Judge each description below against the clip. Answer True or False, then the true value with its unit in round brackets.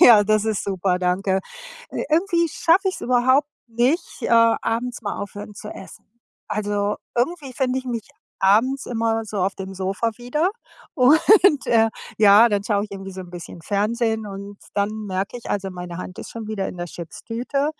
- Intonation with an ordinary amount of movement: True (4.2 semitones)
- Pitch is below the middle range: False (215 Hz)